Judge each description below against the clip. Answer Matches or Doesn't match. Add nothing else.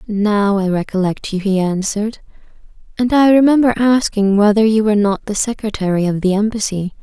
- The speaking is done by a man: Doesn't match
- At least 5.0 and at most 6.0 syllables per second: Matches